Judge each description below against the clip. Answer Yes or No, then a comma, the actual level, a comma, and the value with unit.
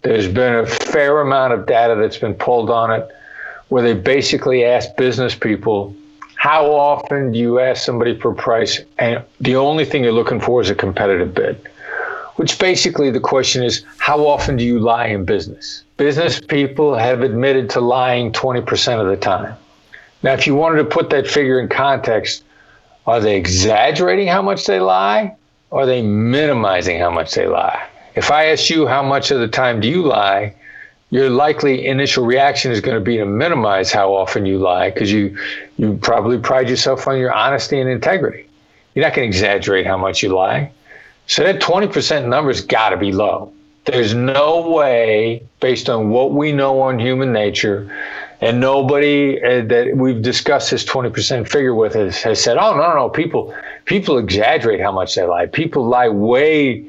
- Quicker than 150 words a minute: Yes, average, 185 wpm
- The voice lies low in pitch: Yes, low, 130 Hz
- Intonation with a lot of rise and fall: No, average, 3.6 semitones